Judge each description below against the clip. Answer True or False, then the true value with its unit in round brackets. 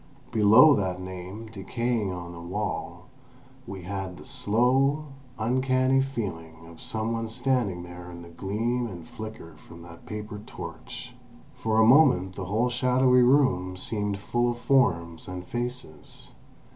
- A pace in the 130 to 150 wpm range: True (145 wpm)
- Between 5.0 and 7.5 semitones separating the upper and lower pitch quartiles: True (5.3 semitones)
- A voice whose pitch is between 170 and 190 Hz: False (105 Hz)